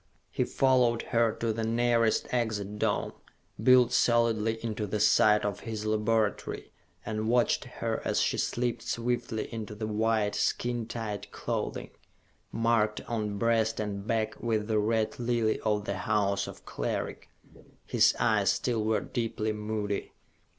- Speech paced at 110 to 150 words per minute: Yes, average, 145 wpm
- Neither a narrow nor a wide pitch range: No, narrow, 1.6 semitones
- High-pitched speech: No, low, 110 Hz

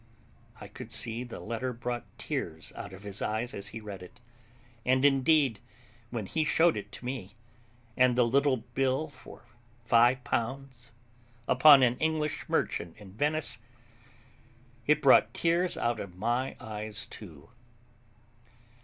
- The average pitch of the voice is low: Yes, low, 120 Hz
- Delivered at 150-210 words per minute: No, average, 140 wpm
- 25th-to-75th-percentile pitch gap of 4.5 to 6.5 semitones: No, average, 4.0 semitones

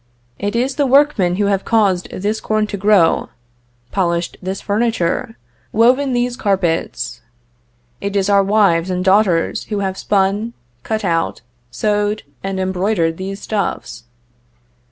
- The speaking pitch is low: No, high, 200 Hz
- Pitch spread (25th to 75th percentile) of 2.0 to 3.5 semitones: Yes, average, 2.9 semitones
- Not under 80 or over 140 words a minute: Yes, slow, 135 wpm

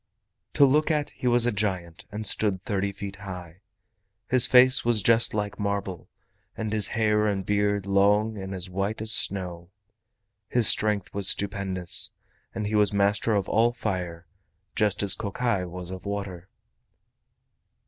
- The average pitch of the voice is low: Yes, low, 100 Hz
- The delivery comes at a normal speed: Yes, average, 155 wpm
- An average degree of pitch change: No, narrow, 2.3 semitones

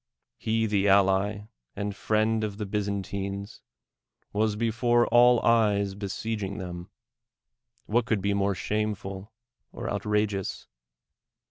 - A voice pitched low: Yes, low, 105 Hz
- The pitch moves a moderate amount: No, narrow, 2.0 semitones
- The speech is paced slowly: Yes, slow, 120 wpm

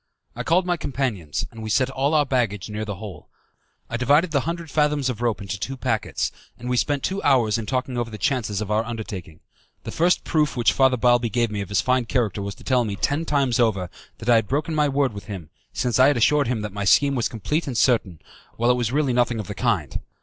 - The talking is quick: Yes, fast, 245 wpm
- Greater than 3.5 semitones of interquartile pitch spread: Yes, average, 4.5 semitones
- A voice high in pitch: No, low, 120 Hz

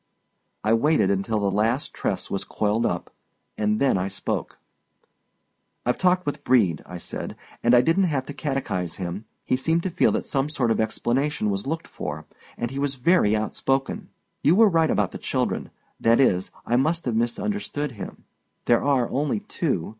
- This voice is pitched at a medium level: No, low, 130 Hz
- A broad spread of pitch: Yes, wide, 5.7 semitones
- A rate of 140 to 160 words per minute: No, average, 175 wpm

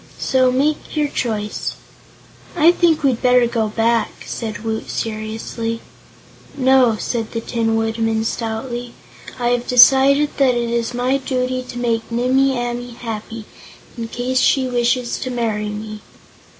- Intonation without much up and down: Yes, narrow, 2.2 semitones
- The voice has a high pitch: Yes, high, 240 Hz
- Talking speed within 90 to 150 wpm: Yes, slow, 135 wpm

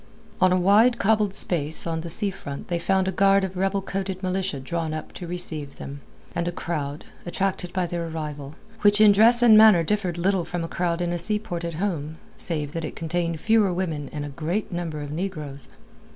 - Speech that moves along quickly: Yes, fast, 210 wpm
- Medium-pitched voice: Yes, medium, 175 Hz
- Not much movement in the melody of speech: No, average, 3.4 semitones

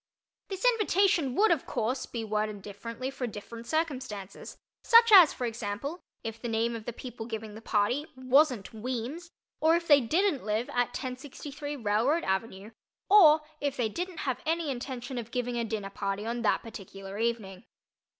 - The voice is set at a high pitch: Yes, high, 245 Hz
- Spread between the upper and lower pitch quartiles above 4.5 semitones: Yes, average, 5.1 semitones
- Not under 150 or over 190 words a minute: Yes, average, 170 wpm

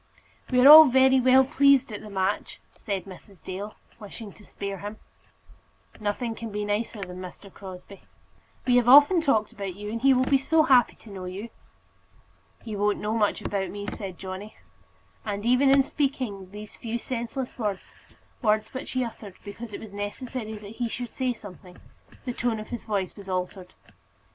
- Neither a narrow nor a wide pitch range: Yes, average, 3.9 semitones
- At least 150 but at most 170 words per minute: No, average, 185 wpm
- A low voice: No, high, 215 Hz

